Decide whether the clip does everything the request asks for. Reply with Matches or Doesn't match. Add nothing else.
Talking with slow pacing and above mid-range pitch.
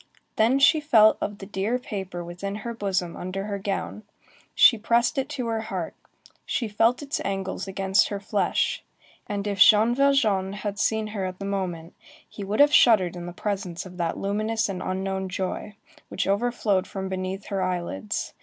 Doesn't match